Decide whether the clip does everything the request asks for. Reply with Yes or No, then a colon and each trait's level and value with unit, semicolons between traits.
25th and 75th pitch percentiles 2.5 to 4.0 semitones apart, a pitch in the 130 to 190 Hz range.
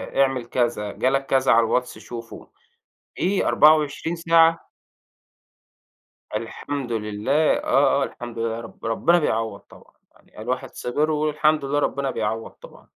No: average, 4.6 semitones; low, 135 Hz